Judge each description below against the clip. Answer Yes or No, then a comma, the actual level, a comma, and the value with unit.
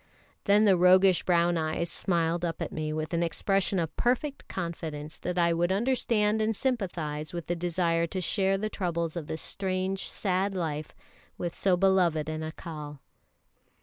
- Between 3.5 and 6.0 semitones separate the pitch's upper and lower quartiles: No, average, 3.0 semitones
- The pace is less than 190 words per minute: Yes, average, 165 wpm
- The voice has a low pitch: No, medium, 175 Hz